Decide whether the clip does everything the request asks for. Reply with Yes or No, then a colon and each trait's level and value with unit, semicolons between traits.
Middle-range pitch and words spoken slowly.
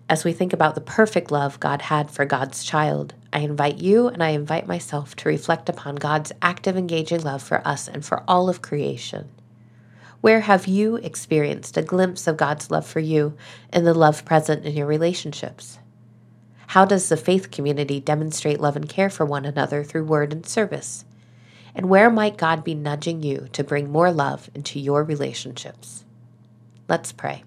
No: medium, 150 Hz; average, 180 wpm